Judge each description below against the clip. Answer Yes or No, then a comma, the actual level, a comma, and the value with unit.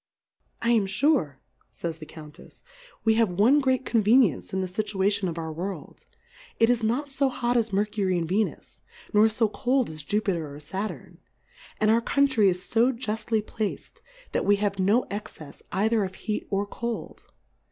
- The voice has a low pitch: No, high, 210 Hz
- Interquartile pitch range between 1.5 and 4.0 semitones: Yes, average, 3.6 semitones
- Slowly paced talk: No, average, 180 wpm